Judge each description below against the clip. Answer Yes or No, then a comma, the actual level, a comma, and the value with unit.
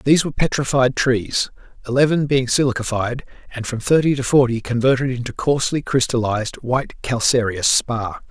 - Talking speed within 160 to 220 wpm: No, slow, 135 wpm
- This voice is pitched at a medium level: No, low, 125 Hz